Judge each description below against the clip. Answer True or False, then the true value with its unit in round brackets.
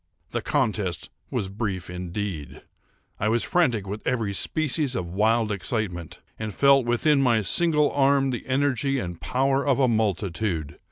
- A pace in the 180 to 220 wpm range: False (150 wpm)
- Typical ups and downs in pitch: False (5.9 semitones)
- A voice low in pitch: True (110 Hz)